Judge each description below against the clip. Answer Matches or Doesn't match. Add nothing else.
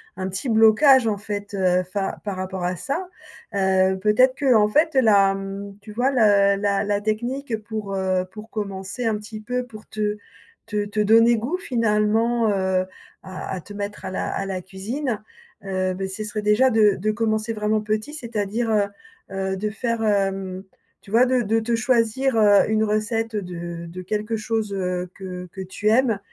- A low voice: Doesn't match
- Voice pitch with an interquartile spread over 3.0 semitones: Doesn't match